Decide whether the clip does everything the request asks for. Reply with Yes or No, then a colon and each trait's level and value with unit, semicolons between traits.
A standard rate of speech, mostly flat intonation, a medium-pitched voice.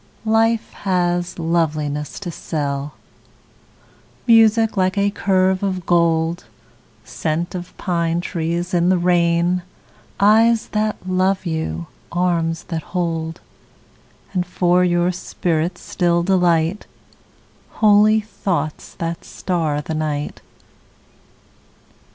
No: slow, 100 wpm; narrow, 2.3 semitones; medium, 175 Hz